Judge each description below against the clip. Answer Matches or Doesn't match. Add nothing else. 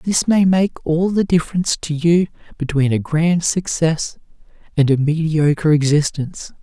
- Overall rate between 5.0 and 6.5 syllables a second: Doesn't match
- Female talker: Doesn't match